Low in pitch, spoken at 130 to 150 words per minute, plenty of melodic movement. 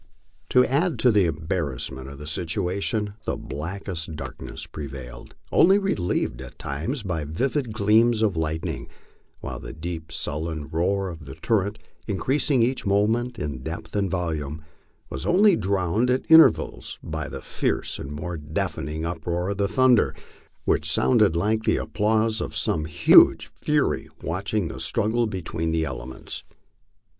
Yes: very low, 90 Hz; average, 145 wpm; wide, 5.8 semitones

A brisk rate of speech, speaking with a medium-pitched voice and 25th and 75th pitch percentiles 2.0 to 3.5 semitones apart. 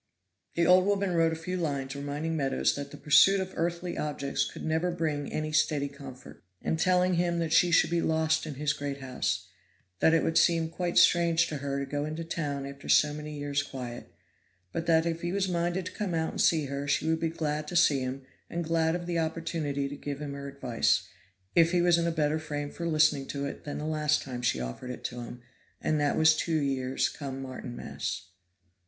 Yes: fast, 220 wpm; medium, 155 Hz; average, 3.1 semitones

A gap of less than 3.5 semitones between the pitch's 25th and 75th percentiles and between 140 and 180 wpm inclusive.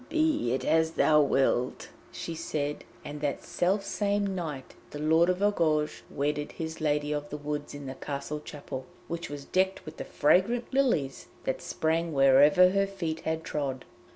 No: average, 3.9 semitones; average, 170 wpm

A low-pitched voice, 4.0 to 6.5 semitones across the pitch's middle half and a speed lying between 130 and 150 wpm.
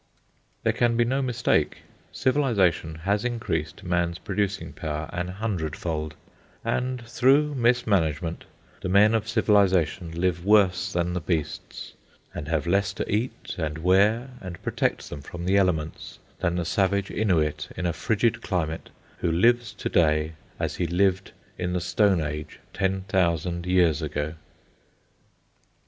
Yes: very low, 90 Hz; average, 4.3 semitones; average, 145 wpm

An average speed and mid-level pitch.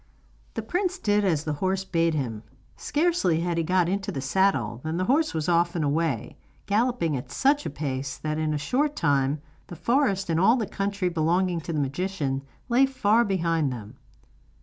Yes: average, 190 wpm; medium, 170 Hz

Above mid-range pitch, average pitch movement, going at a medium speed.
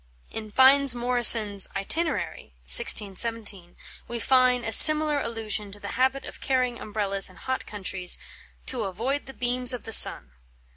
Yes: high, 230 Hz; average, 4.1 semitones; average, 145 wpm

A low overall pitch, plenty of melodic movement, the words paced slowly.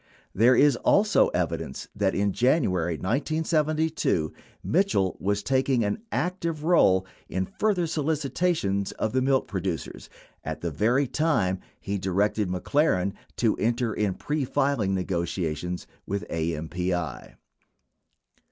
Yes: low, 105 Hz; wide, 8.2 semitones; slow, 125 wpm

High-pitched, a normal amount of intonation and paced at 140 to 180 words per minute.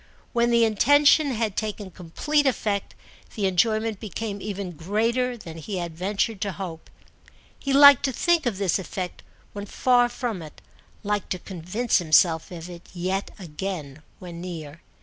Yes: high, 200 Hz; average, 4.9 semitones; average, 155 wpm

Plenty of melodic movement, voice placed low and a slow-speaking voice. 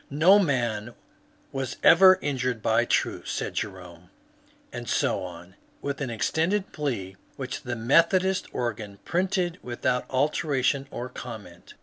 Yes: wide, 6.3 semitones; low, 130 Hz; slow, 130 wpm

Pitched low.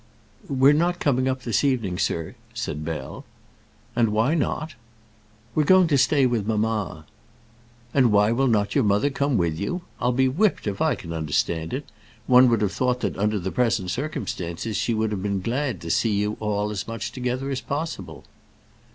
Yes: low, 115 Hz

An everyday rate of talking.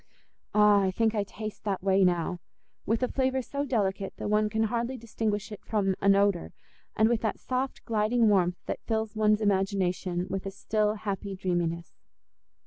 Yes: average, 170 wpm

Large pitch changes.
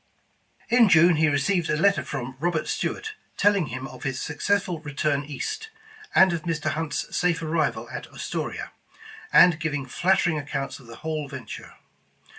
No: average, 3.8 semitones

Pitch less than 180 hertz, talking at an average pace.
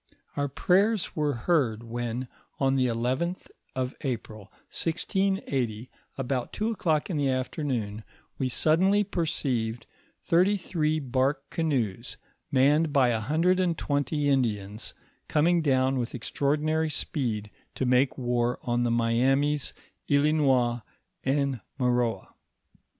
No: low, 135 Hz; slow, 115 wpm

